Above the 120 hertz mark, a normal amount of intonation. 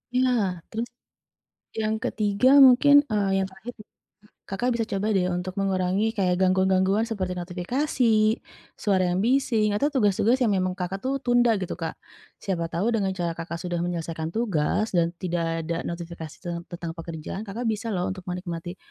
Yes: high, 190 Hz; average, 3.9 semitones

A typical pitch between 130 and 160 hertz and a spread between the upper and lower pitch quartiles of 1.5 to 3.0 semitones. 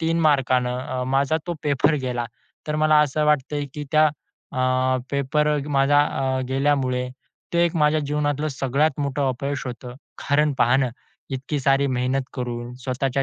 Yes: medium, 140 Hz; narrow, 2.6 semitones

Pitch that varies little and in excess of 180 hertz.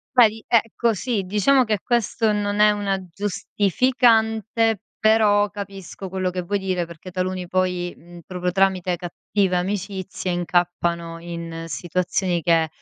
No: average, 3.0 semitones; high, 190 Hz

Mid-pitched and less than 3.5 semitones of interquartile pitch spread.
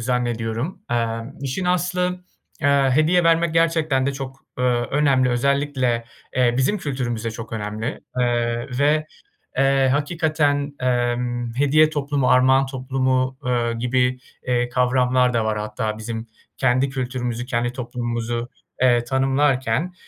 No: low, 130 Hz; average, 2.8 semitones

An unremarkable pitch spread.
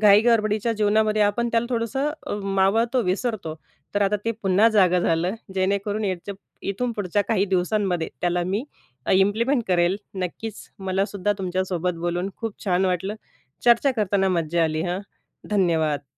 Yes: average, 3.1 semitones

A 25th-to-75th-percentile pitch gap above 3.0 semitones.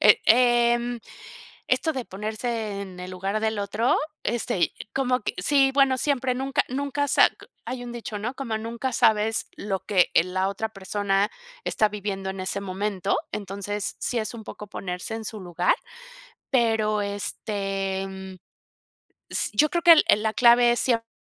Yes: average, 3.6 semitones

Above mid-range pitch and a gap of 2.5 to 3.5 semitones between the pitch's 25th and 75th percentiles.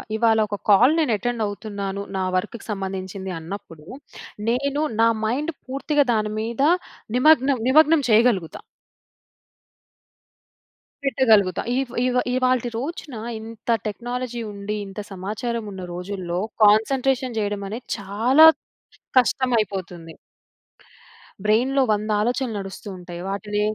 No: high, 220 Hz; average, 4.1 semitones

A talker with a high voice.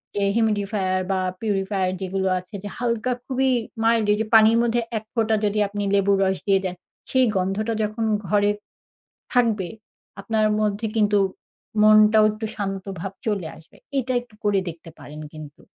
Yes: high, 205 Hz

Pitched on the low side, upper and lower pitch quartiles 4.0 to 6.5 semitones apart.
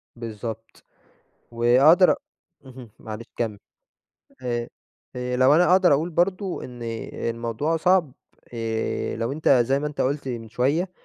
Yes: low, 125 Hz; average, 5.1 semitones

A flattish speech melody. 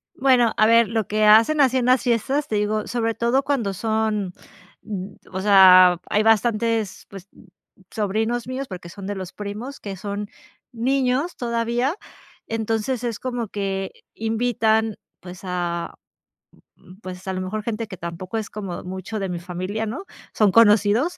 No: average, 3.4 semitones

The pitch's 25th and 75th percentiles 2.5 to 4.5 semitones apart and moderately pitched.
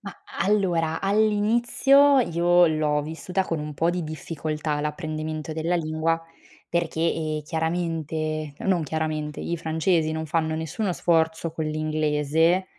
No: narrow, 1.9 semitones; medium, 160 Hz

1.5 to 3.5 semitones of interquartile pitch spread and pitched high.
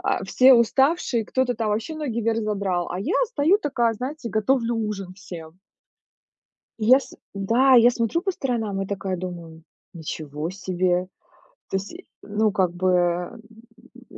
No: average, 5.0 semitones; high, 215 Hz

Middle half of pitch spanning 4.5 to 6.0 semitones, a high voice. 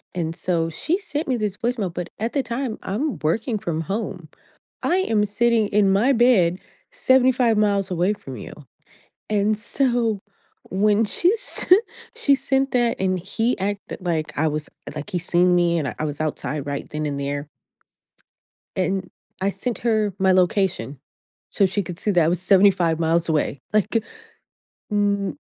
Yes: average, 5.0 semitones; high, 200 Hz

